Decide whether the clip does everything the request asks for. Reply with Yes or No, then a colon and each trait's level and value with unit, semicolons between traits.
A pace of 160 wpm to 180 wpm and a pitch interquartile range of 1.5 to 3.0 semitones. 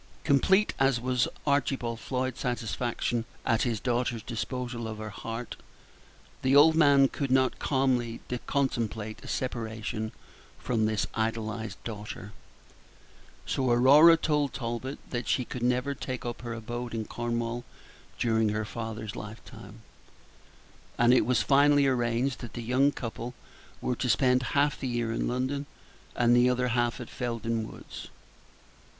No: average, 140 wpm; narrow, 2.4 semitones